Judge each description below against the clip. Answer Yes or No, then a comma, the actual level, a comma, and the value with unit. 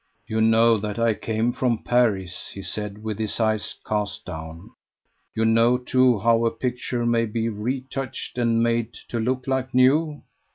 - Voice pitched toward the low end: Yes, low, 115 Hz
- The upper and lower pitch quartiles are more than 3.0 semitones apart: No, narrow, 2.4 semitones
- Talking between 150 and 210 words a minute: Yes, average, 165 wpm